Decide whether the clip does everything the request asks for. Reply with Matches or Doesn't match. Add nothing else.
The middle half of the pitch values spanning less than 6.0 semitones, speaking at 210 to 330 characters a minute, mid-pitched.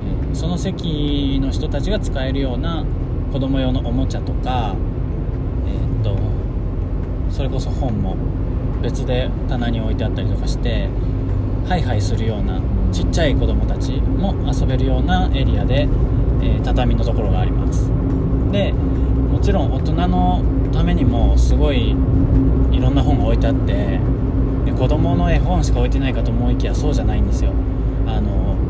Doesn't match